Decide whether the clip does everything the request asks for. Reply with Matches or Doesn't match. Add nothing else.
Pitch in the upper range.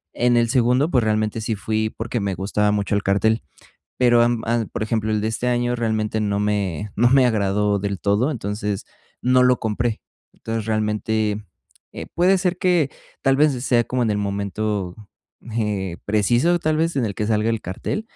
Doesn't match